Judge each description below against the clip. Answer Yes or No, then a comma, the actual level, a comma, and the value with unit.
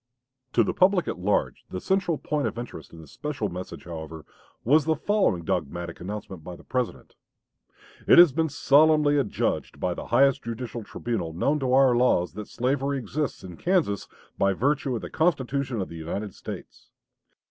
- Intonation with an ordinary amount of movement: No, wide, 7.6 semitones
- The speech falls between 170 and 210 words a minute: Yes, average, 175 wpm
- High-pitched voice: No, low, 125 Hz